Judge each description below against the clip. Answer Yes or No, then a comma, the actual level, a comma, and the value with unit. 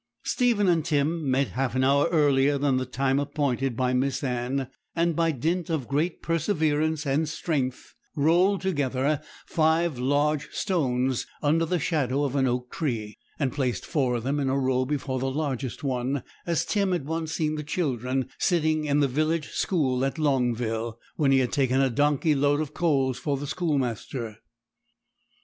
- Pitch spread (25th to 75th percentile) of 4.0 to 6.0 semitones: No, average, 3.3 semitones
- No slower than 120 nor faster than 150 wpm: No, average, 170 wpm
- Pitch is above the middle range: No, medium, 140 Hz